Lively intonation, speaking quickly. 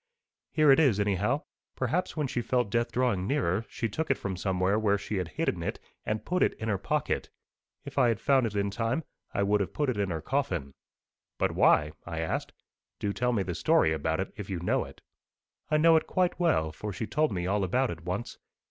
Yes: wide, 6.0 semitones; fast, 225 wpm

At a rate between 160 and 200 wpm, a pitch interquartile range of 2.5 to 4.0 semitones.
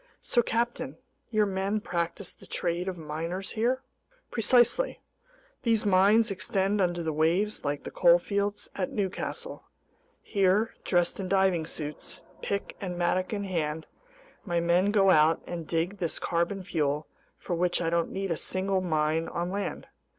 No: average, 150 wpm; average, 3.2 semitones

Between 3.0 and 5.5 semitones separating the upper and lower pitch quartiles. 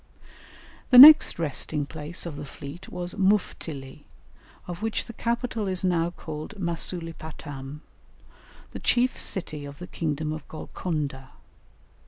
Yes: average, 4.3 semitones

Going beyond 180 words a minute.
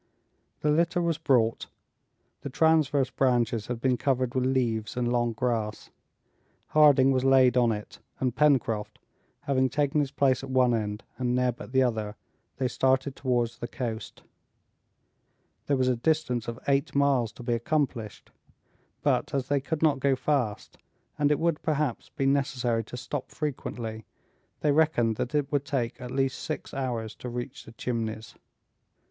No: average, 165 wpm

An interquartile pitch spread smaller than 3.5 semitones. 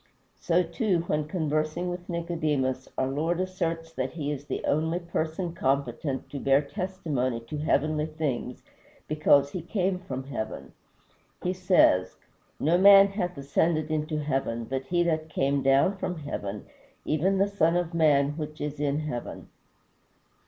No: average, 3.8 semitones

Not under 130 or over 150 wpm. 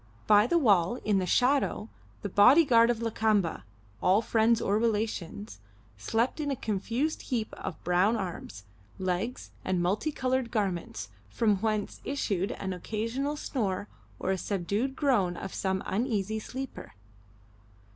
Yes: average, 140 wpm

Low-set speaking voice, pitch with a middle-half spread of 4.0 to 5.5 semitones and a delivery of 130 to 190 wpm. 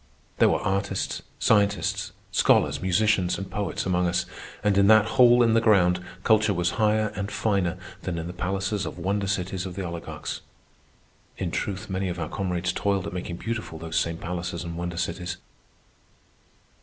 No: very low, 95 Hz; average, 2.7 semitones; average, 170 wpm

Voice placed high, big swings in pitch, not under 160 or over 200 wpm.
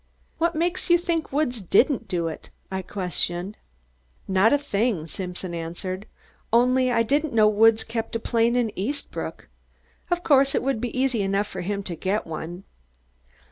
Yes: high, 225 Hz; wide, 5.8 semitones; average, 165 wpm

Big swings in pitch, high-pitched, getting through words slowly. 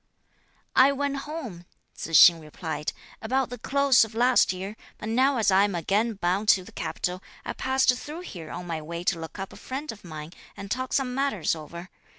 No: wide, 7.0 semitones; high, 210 Hz; average, 200 wpm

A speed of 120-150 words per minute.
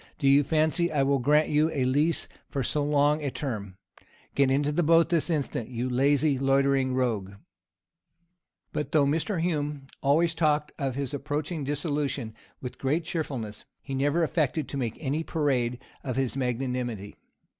No: average, 160 wpm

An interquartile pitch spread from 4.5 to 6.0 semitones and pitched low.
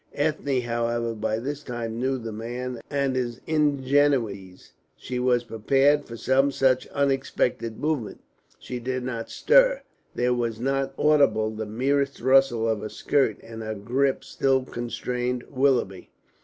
No: average, 3.0 semitones; low, 125 Hz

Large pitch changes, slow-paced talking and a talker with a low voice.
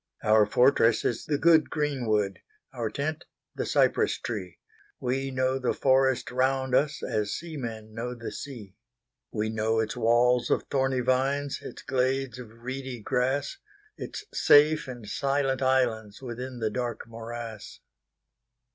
No: average, 3.0 semitones; slow, 115 wpm; low, 125 Hz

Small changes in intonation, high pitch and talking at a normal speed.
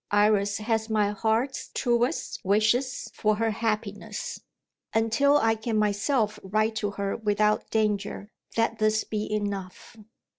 No: narrow, 1.4 semitones; high, 215 Hz; slow, 125 wpm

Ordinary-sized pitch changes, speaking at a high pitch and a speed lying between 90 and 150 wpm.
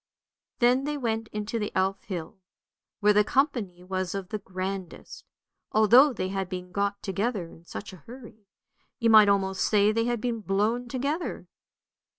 No: average, 3.5 semitones; high, 210 Hz; average, 160 wpm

